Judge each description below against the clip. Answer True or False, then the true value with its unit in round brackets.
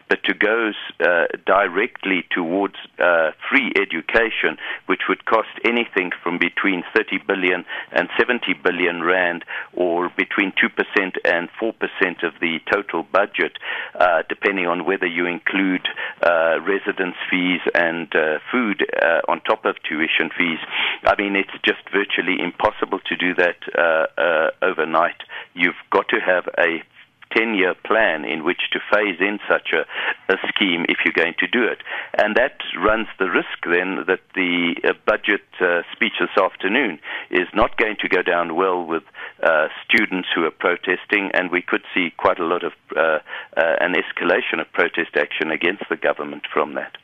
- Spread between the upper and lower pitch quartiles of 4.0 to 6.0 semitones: False (3.5 semitones)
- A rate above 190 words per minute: False (165 wpm)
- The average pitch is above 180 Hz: False (90 Hz)